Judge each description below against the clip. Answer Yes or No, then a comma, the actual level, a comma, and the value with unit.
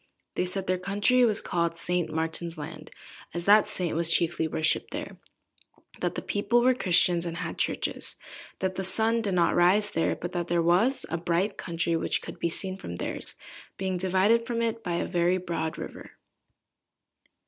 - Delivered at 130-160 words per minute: No, average, 180 wpm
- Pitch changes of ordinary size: Yes, average, 3.2 semitones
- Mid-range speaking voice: Yes, medium, 180 Hz